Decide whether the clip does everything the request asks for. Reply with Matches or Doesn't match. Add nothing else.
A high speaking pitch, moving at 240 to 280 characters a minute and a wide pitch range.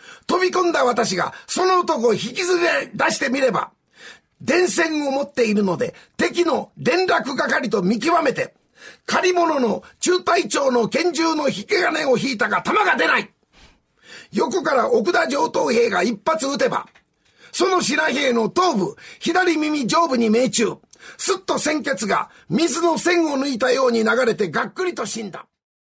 Matches